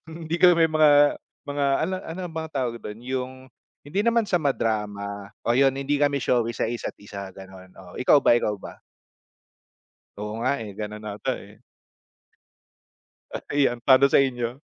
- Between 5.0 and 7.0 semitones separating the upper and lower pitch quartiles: Yes, wide, 5.5 semitones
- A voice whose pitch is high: No, low, 130 Hz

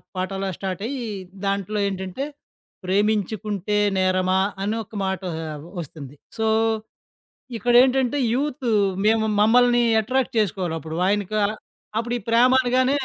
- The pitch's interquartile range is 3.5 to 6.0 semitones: Yes, average, 4.3 semitones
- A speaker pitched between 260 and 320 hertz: No, high, 210 Hz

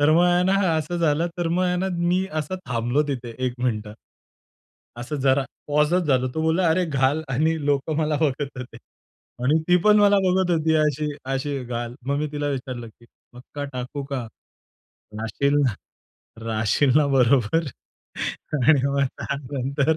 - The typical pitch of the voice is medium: Yes, medium, 145 Hz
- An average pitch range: Yes, average, 3.9 semitones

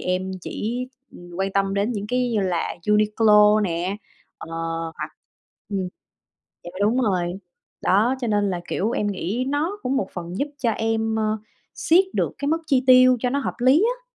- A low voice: No, high, 215 Hz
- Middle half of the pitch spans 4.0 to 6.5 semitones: Yes, average, 4.5 semitones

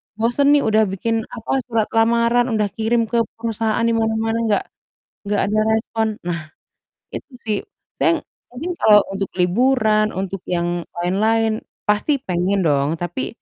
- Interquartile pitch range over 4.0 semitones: No, average, 2.9 semitones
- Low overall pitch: No, high, 220 Hz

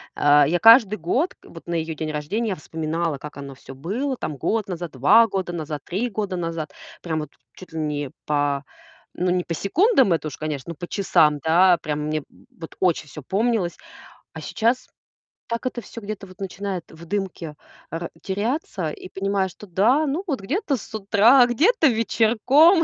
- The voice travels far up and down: Yes, wide, 6.4 semitones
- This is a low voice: No, medium, 185 Hz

